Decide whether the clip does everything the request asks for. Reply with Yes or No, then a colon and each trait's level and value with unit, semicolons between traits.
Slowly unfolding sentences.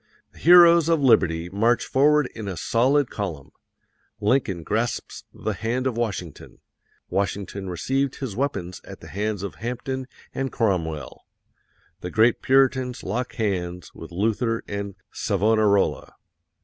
Yes: slow, 130 wpm